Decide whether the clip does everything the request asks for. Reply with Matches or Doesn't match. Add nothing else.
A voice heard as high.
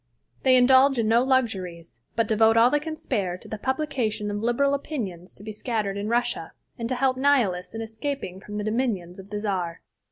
Matches